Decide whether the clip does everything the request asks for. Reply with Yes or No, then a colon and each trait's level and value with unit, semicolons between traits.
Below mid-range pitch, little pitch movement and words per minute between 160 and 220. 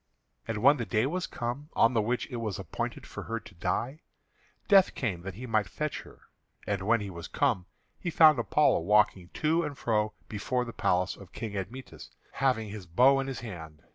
No: low, 115 Hz; average, 5.1 semitones; average, 200 wpm